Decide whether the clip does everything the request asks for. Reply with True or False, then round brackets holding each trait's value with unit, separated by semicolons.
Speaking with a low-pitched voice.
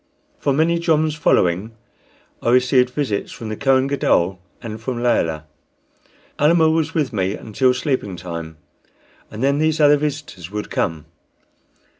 True (125 Hz)